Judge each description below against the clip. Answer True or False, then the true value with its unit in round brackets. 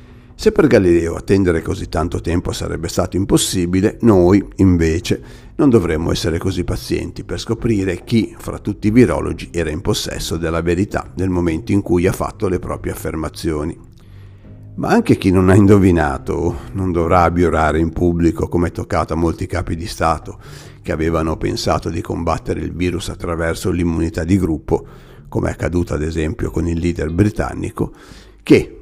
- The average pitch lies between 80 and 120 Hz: True (90 Hz)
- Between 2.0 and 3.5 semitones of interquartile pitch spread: True (3.2 semitones)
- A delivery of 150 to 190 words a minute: True (160 wpm)